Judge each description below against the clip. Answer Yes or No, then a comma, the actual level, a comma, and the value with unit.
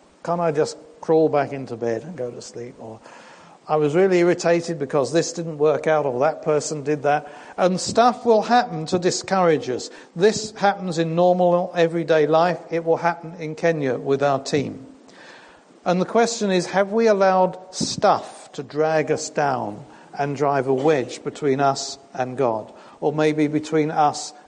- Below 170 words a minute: No, average, 175 wpm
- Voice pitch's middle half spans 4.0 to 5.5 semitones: No, average, 3.4 semitones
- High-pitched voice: No, medium, 160 Hz